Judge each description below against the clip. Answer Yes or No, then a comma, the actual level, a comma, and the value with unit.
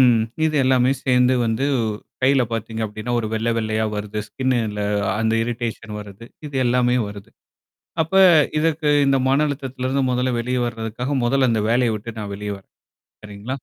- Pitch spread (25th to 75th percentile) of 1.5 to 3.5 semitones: Yes, average, 2.9 semitones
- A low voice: Yes, low, 120 Hz